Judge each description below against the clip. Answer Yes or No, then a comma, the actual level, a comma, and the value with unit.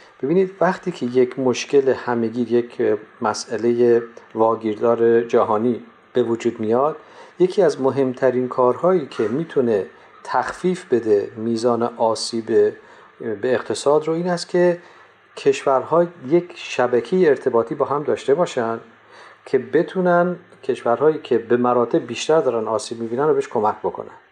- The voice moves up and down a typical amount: No, wide, 7.3 semitones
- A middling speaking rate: Yes, average, 125 wpm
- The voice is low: Yes, low, 130 Hz